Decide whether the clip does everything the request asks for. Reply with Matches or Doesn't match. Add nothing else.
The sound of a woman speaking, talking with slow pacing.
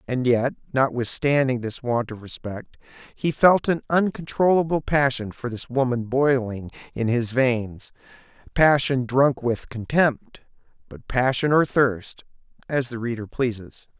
Doesn't match